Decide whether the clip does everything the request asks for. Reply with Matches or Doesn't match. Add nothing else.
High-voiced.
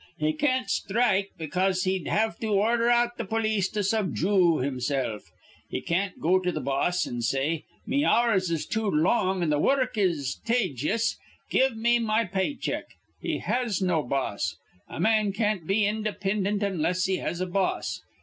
Matches